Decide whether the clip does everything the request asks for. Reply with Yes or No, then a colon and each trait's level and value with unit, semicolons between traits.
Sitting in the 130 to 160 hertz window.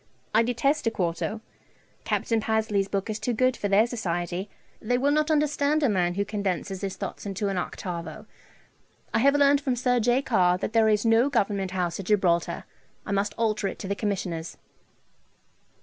No: high, 210 Hz